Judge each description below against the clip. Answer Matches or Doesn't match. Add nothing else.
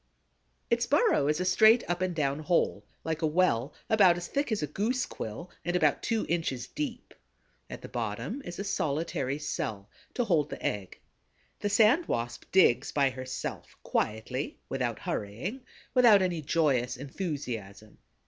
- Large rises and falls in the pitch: Matches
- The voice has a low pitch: Doesn't match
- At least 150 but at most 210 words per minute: Matches